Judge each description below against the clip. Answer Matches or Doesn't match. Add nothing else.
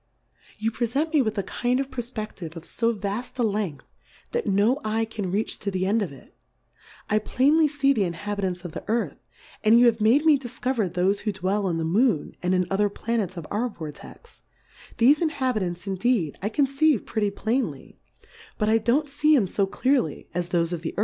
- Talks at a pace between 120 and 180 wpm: Doesn't match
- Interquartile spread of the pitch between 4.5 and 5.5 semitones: Matches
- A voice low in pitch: Doesn't match